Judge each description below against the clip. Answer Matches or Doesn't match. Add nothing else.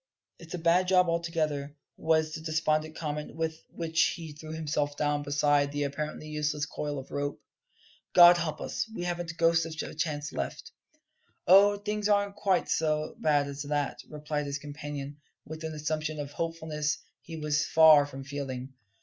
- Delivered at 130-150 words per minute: Doesn't match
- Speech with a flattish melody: Matches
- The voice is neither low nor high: Matches